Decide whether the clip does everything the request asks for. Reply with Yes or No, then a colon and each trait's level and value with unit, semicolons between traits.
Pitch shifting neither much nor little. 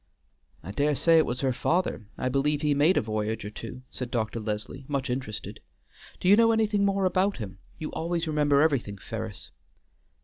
No: wide, 6.9 semitones